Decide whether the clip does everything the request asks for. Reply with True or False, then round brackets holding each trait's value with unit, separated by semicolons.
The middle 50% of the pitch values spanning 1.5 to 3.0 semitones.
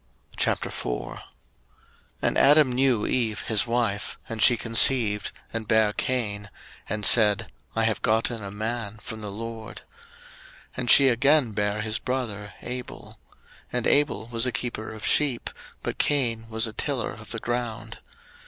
True (2.4 semitones)